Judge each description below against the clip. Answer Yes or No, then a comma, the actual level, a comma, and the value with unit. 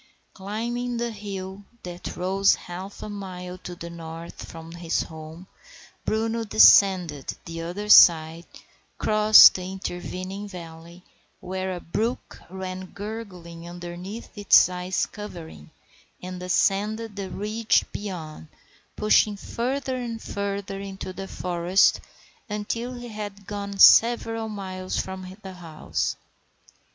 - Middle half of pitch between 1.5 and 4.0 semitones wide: Yes, average, 3.0 semitones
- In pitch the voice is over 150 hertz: Yes, high, 190 Hz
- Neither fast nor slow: No, slow, 120 wpm